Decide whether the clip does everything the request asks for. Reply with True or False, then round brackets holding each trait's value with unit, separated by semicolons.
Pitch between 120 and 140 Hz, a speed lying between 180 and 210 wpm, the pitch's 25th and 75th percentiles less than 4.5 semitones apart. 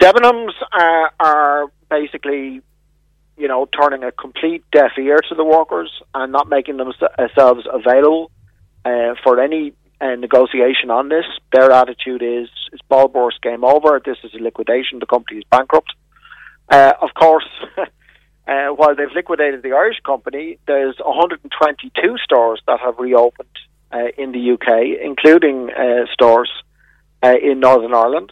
False (135 Hz; 145 wpm; 3.8 semitones)